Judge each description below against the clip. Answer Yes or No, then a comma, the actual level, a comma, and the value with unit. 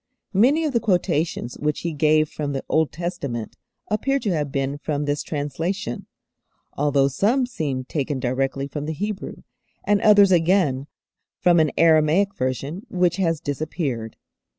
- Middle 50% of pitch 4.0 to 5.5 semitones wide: Yes, average, 5.0 semitones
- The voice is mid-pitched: Yes, medium, 155 Hz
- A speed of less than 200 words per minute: Yes, average, 150 wpm